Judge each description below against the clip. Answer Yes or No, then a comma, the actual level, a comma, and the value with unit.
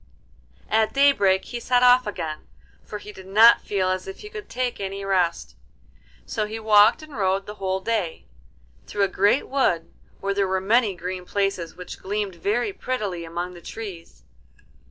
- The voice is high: Yes, high, 200 Hz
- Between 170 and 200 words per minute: Yes, average, 175 wpm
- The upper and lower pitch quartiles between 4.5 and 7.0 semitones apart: No, average, 3.2 semitones